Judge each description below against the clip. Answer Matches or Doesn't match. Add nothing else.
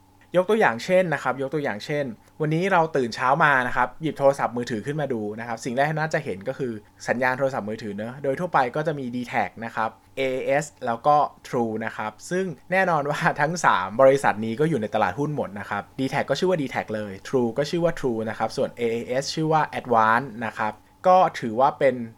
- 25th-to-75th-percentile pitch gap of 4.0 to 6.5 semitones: Matches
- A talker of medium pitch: Doesn't match